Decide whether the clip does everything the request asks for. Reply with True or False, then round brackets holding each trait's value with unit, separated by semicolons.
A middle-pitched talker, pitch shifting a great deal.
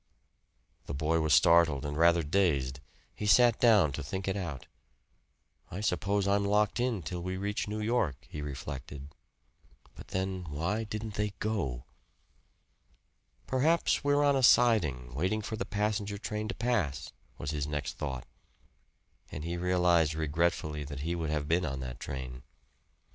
False (85 Hz; 6.2 semitones)